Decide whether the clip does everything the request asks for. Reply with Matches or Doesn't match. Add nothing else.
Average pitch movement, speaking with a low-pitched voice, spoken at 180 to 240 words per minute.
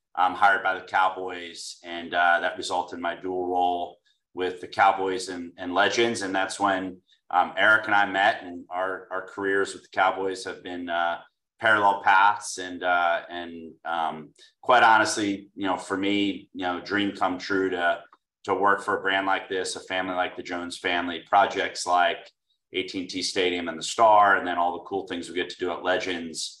Doesn't match